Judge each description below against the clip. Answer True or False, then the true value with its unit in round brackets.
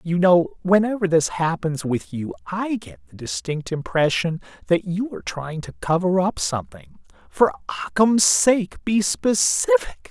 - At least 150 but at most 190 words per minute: False (140 wpm)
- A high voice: False (160 Hz)